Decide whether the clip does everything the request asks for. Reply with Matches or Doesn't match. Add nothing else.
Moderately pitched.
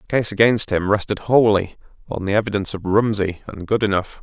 Doesn't match